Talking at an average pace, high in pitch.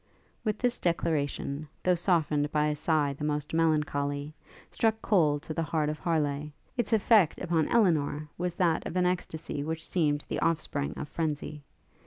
No: average, 165 wpm; medium, 155 Hz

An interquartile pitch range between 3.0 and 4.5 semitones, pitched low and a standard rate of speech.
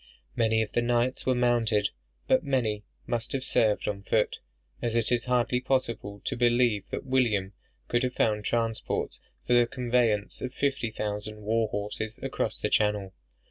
No: narrow, 2.6 semitones; low, 115 Hz; average, 165 wpm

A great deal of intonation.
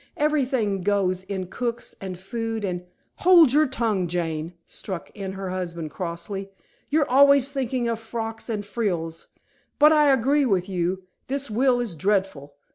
Yes: wide, 5.9 semitones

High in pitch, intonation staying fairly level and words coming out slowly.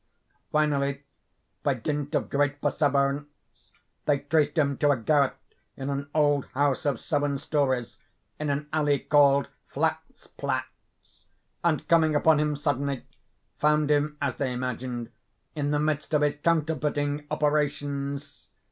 No: medium, 145 Hz; narrow, 1.2 semitones; slow, 130 wpm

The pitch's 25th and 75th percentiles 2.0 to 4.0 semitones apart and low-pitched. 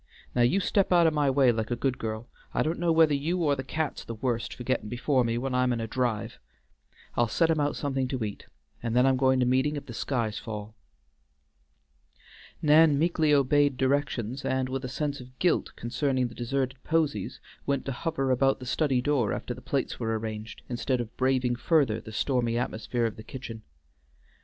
Yes: average, 3.3 semitones; low, 130 Hz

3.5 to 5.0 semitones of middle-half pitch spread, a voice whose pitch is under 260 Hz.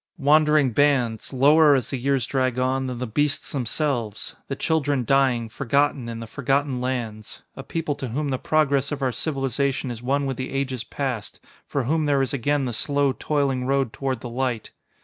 No: narrow, 2.4 semitones; low, 135 Hz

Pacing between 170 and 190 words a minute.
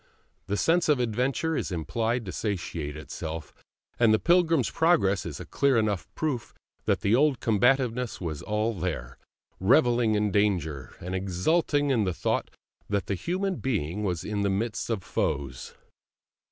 No: average, 155 wpm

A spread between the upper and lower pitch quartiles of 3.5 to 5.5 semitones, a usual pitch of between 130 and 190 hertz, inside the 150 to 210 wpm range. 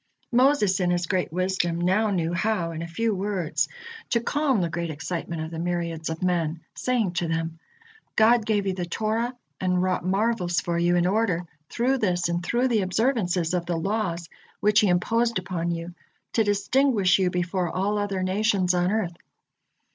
Yes: average, 3.8 semitones; medium, 185 Hz; average, 180 wpm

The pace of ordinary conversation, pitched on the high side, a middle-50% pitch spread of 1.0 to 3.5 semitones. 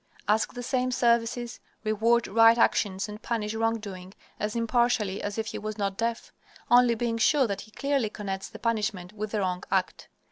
Yes: average, 180 wpm; high, 220 Hz; narrow, 2.4 semitones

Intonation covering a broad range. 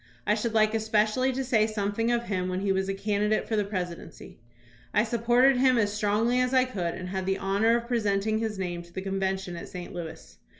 No: average, 3.1 semitones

